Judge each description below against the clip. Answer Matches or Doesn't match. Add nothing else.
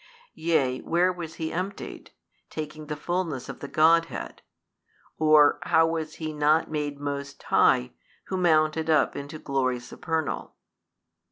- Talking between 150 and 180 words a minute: Doesn't match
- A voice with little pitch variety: Matches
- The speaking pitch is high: Doesn't match